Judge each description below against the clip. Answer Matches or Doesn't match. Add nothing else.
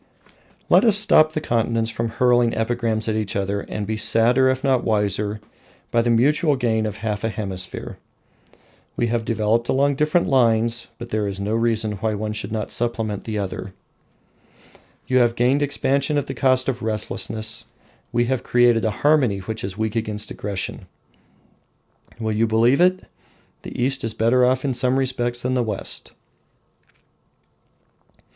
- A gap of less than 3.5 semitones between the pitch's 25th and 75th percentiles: Matches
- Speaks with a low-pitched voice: Matches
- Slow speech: Doesn't match